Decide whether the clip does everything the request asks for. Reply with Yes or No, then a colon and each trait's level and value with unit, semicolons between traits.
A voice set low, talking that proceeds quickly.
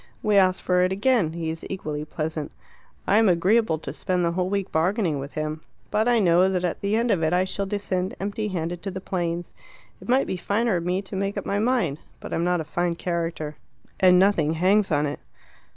No: medium, 180 Hz; fast, 220 wpm